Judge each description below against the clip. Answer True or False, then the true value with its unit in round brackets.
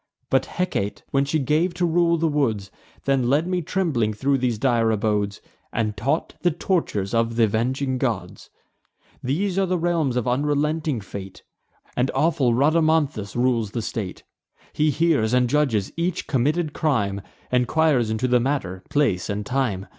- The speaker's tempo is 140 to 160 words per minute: True (155 wpm)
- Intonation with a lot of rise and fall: True (6.0 semitones)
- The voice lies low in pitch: True (130 Hz)